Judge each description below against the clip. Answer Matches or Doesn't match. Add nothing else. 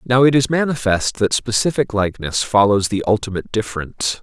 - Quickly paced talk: Doesn't match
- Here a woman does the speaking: Doesn't match